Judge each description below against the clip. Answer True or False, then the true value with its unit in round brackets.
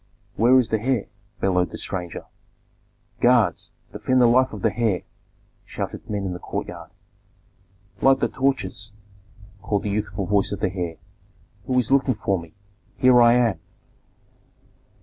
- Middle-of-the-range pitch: False (110 Hz)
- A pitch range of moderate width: True (4.5 semitones)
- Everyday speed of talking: True (150 wpm)